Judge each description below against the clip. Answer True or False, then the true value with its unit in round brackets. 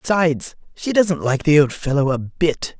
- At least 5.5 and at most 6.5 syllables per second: False (4.7 syllables/s)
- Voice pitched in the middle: True (155 Hz)